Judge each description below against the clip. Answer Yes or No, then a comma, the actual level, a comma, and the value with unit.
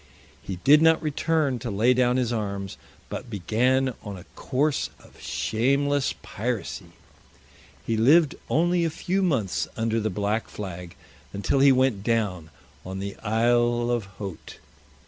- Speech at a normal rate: Yes, average, 145 wpm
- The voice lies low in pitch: Yes, low, 120 Hz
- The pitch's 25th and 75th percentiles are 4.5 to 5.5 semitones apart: Yes, average, 5.1 semitones